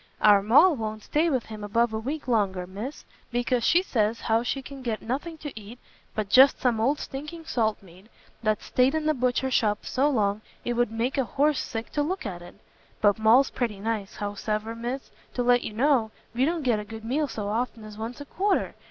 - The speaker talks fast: Yes, fast, 215 wpm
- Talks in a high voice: Yes, high, 235 Hz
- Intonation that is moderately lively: Yes, average, 4.0 semitones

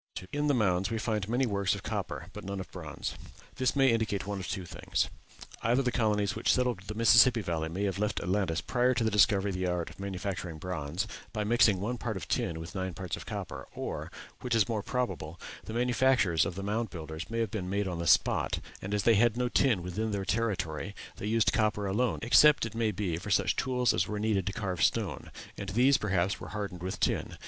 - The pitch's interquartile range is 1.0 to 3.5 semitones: No, average, 3.9 semitones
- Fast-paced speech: Yes, fast, 225 wpm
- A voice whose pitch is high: No, low, 105 Hz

